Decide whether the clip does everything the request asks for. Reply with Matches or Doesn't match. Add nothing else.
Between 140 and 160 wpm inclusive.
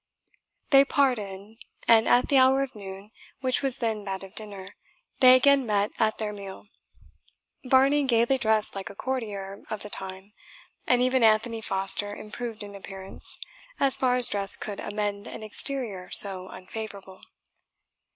Matches